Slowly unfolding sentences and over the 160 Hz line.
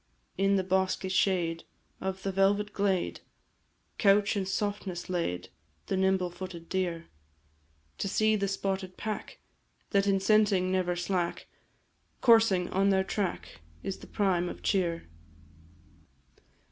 Yes: slow, 125 wpm; high, 190 Hz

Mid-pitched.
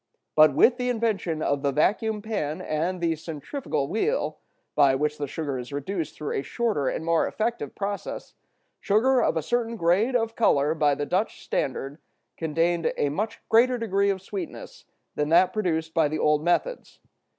Yes: medium, 170 Hz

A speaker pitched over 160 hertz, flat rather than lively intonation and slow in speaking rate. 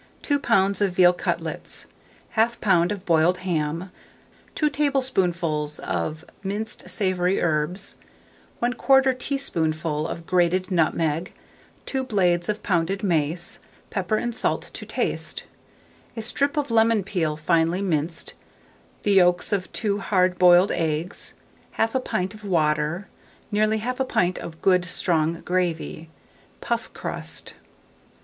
No: medium, 185 Hz; average, 4.2 semitones; slow, 125 wpm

